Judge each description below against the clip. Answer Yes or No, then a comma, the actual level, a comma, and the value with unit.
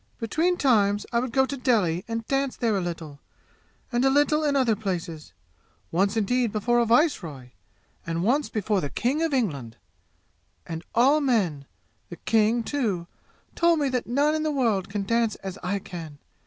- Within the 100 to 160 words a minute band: No, average, 175 wpm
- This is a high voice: Yes, high, 225 Hz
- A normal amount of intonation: No, wide, 6.4 semitones